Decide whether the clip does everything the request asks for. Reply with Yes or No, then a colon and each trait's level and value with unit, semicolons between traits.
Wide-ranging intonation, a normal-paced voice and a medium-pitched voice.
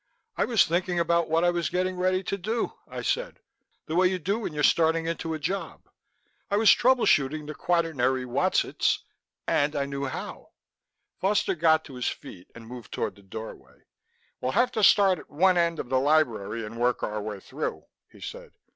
Yes: wide, 6.0 semitones; average, 195 wpm; medium, 160 Hz